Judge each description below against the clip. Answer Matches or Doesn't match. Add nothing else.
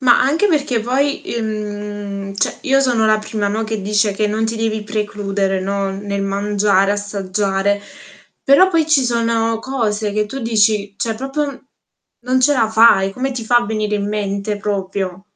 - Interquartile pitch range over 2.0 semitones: Matches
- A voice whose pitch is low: Doesn't match